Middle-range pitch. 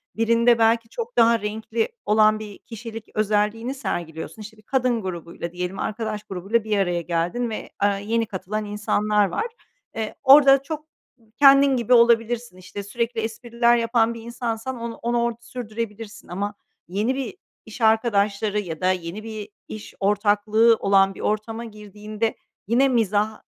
No: high, 220 Hz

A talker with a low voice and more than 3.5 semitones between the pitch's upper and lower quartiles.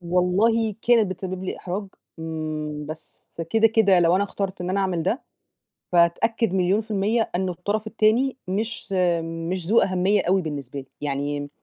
No: medium, 185 Hz; average, 4.2 semitones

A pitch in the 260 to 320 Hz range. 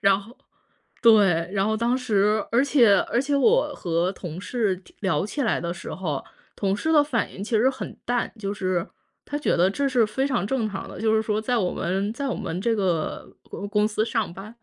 No: high, 215 Hz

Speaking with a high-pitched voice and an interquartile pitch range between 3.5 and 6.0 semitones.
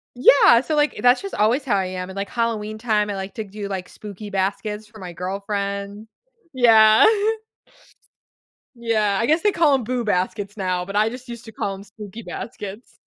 No: high, 210 Hz; average, 2.9 semitones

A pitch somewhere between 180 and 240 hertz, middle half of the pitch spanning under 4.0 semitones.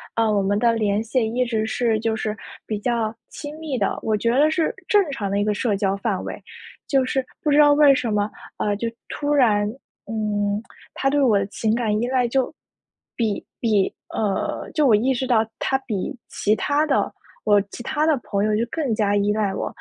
No: high, 225 Hz; average, 4.3 semitones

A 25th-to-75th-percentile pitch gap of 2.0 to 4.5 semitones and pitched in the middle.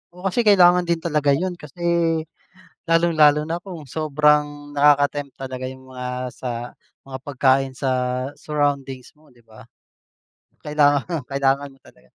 Yes: average, 3.2 semitones; medium, 145 Hz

